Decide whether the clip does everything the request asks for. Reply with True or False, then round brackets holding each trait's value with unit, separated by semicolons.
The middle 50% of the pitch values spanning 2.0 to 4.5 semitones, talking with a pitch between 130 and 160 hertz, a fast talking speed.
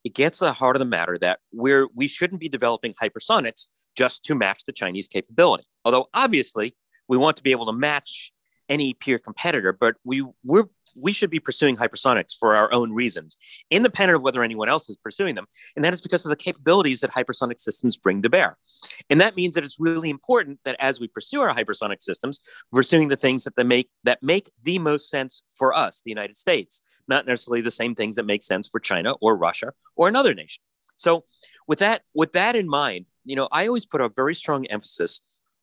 False (5.0 semitones; 135 Hz; 215 wpm)